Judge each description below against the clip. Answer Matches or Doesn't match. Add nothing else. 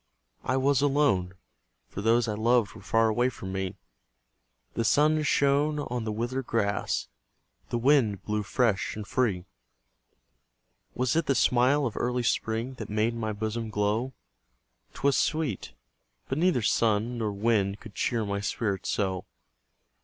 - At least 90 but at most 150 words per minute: Matches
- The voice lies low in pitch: Matches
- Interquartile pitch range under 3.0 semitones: Doesn't match